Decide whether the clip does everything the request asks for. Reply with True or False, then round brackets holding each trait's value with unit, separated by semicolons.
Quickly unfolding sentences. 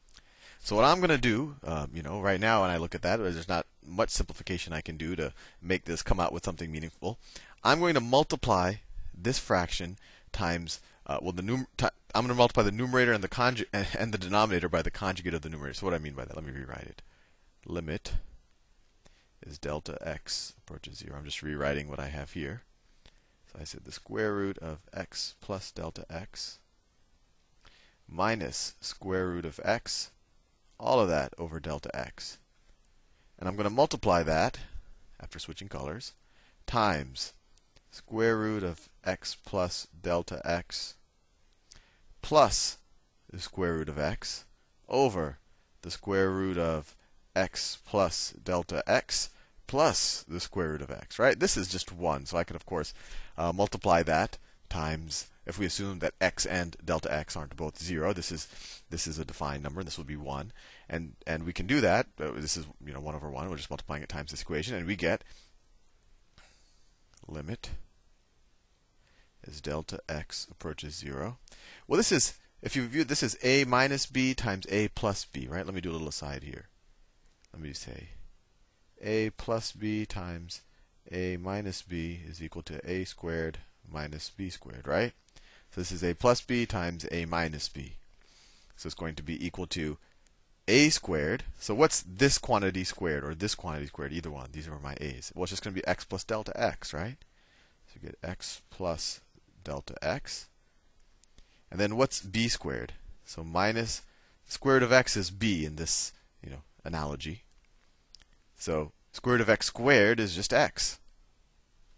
True (180 wpm)